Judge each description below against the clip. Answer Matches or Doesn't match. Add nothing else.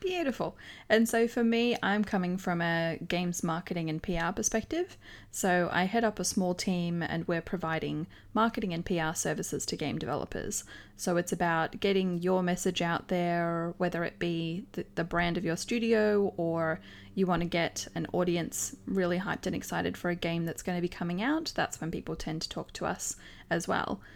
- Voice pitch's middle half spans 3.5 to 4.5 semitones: Doesn't match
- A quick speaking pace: Doesn't match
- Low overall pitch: Doesn't match